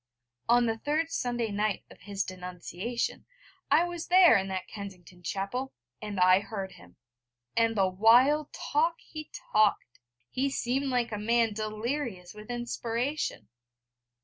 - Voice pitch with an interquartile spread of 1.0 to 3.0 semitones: No, average, 4.8 semitones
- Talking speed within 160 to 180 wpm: No, average, 140 wpm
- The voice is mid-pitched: No, high, 225 Hz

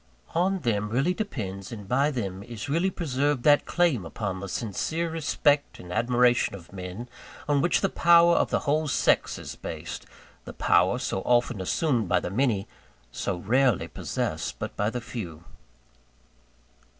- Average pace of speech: Yes, average, 160 wpm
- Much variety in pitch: Yes, wide, 6.9 semitones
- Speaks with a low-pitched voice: Yes, low, 125 Hz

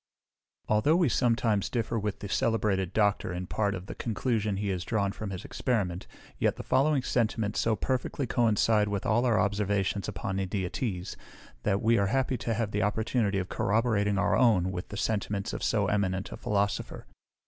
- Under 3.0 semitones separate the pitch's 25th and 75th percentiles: Yes, narrow, 2.6 semitones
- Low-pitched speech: Yes, low, 105 Hz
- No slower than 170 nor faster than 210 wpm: Yes, average, 180 wpm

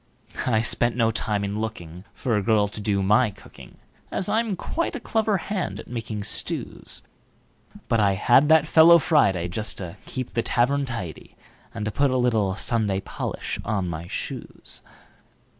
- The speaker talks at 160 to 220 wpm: No, average, 145 wpm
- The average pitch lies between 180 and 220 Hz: No, low, 110 Hz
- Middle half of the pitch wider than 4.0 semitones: Yes, average, 5.2 semitones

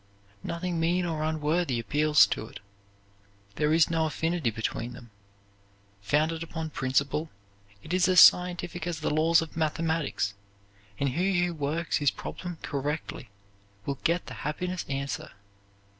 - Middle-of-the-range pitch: Yes, medium, 160 Hz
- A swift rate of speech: No, average, 140 wpm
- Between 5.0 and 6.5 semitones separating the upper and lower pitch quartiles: No, average, 3.1 semitones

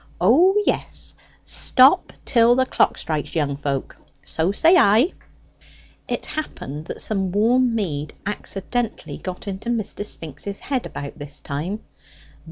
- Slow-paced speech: Yes, slow, 130 wpm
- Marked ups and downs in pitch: Yes, wide, 7.6 semitones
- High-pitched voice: Yes, high, 200 Hz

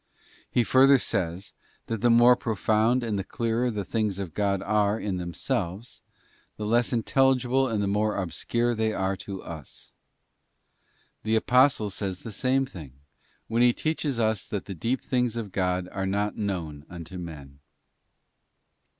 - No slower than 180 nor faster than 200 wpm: No, average, 155 wpm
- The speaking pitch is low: Yes, low, 105 Hz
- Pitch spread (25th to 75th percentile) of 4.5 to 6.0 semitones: No, average, 3.9 semitones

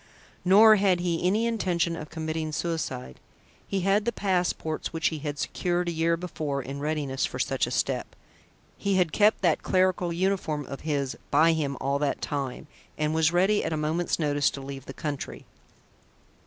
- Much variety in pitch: No, average, 3.6 semitones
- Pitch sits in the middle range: Yes, medium, 160 Hz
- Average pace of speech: Yes, average, 180 wpm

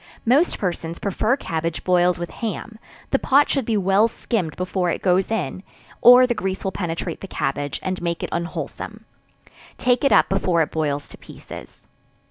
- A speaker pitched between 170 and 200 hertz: Yes, medium, 185 Hz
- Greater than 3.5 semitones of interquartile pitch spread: Yes, average, 4.8 semitones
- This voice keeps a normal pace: Yes, average, 175 wpm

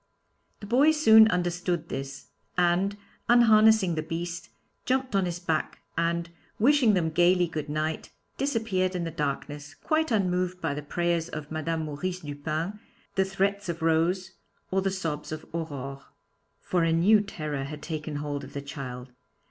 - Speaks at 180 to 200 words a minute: No, average, 155 wpm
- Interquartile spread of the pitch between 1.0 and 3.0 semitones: No, average, 4.0 semitones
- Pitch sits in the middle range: Yes, medium, 170 Hz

